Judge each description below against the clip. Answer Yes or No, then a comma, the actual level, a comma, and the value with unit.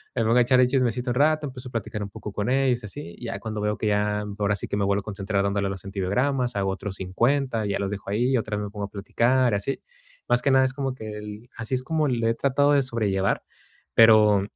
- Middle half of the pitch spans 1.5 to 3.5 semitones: No, average, 3.9 semitones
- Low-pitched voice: Yes, low, 110 Hz